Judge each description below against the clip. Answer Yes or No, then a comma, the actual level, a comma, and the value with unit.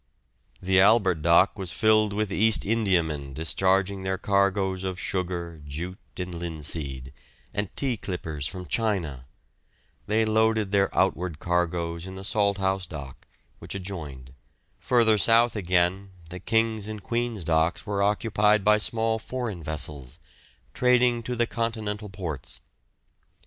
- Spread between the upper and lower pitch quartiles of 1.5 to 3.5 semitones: No, average, 4.1 semitones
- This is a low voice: Yes, very low, 95 Hz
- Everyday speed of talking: No, slow, 130 wpm